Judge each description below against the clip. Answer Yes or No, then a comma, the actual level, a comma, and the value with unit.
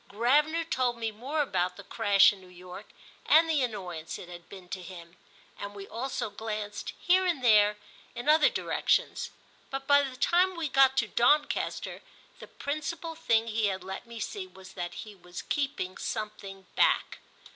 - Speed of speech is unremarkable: Yes, average, 175 wpm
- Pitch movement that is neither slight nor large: No, wide, 6.8 semitones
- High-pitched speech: Yes, high, 225 Hz